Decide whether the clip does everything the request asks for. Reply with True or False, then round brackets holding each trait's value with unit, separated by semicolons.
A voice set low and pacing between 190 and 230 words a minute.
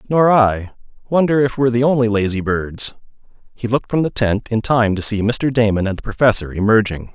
True (115 Hz; 200 wpm)